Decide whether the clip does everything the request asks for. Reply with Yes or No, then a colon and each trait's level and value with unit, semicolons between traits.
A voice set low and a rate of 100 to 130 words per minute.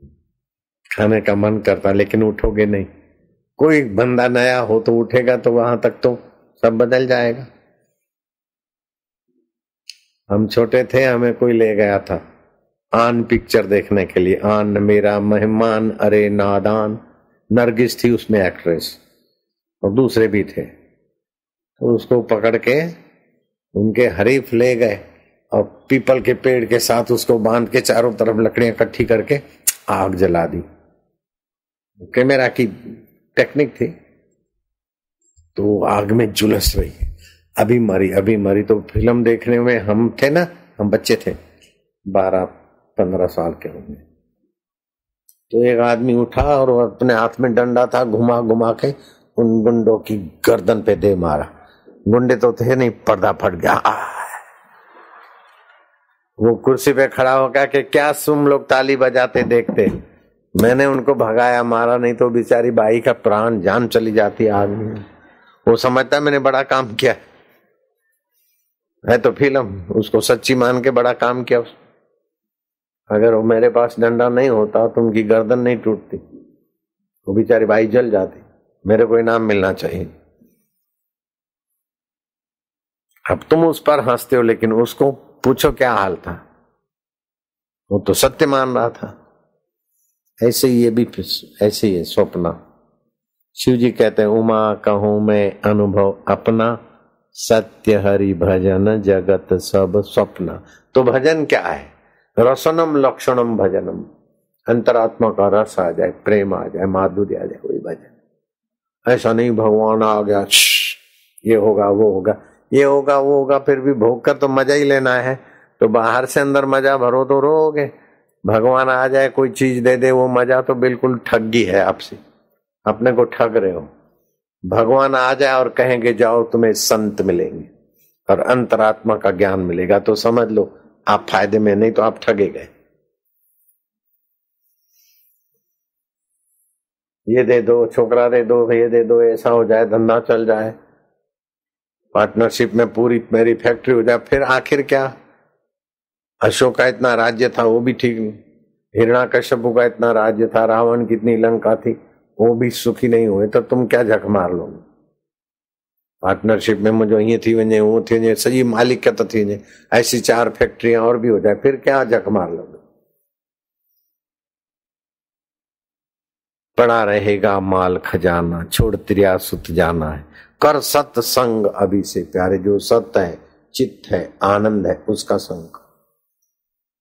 No: low, 115 Hz; average, 145 wpm